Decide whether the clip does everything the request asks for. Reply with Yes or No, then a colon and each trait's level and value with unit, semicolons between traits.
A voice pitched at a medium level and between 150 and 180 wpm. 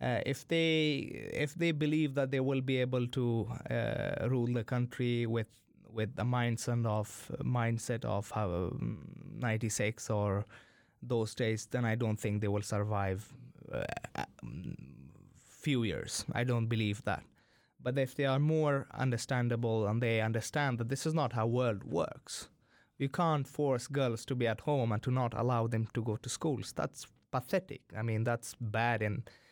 No: low, 120 Hz; average, 170 wpm